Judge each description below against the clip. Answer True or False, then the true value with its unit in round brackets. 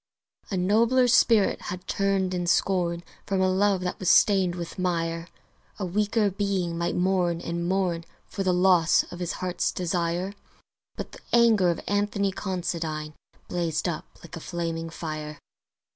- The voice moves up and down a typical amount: False (2.3 semitones)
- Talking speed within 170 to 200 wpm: False (155 wpm)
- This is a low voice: False (180 Hz)